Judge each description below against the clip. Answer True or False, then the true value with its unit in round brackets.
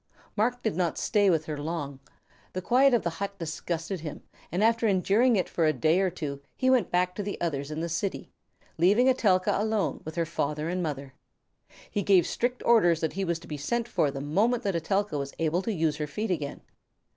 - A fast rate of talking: True (215 wpm)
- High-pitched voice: False (180 Hz)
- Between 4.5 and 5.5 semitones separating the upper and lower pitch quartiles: True (4.9 semitones)